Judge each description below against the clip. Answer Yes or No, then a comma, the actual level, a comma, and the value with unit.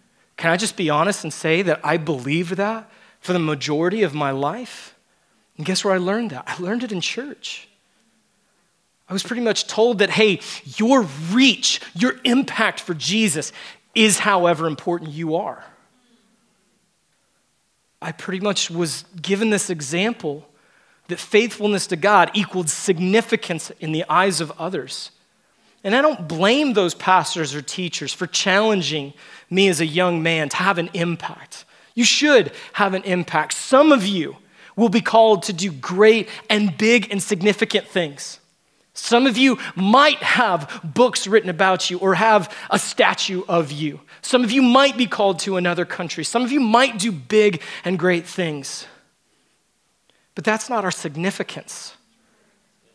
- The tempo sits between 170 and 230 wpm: No, average, 160 wpm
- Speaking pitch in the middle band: No, high, 195 Hz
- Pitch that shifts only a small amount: No, average, 4.4 semitones